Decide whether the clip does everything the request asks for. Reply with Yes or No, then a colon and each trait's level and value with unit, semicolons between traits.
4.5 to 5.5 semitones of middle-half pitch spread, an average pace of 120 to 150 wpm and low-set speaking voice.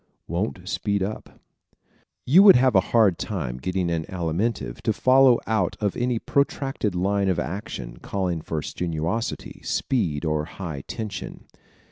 Yes: average, 5.2 semitones; average, 140 wpm; very low, 95 Hz